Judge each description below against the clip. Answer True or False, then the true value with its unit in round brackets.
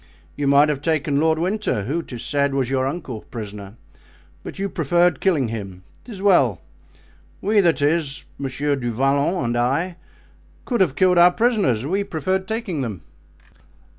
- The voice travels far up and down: True (5.7 semitones)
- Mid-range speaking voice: True (145 Hz)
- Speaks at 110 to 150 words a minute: True (145 wpm)